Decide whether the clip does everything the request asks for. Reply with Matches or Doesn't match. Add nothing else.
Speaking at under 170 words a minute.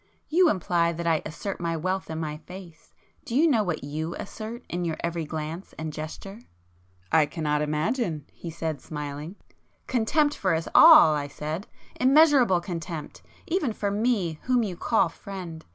Matches